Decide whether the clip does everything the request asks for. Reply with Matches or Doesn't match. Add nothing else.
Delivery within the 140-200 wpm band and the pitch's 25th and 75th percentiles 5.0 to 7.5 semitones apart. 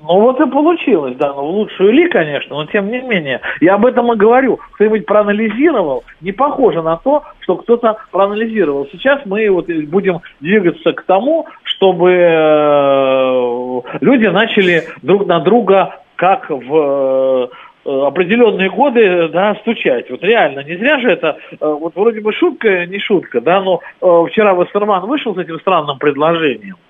Matches